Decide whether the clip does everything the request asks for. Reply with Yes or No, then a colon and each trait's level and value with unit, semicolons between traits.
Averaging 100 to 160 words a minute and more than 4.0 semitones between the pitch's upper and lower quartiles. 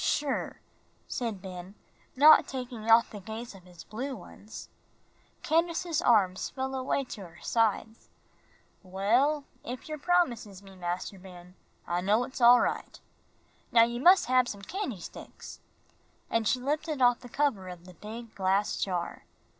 Yes: average, 150 wpm; wide, 5.5 semitones